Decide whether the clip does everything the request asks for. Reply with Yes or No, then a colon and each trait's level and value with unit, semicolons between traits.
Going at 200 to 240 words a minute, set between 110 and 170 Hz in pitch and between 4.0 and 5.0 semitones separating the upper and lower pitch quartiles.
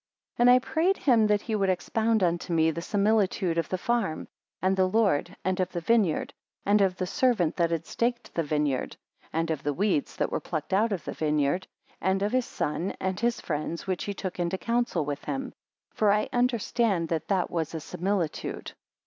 No: fast, 205 wpm; high, 190 Hz; average, 4.7 semitones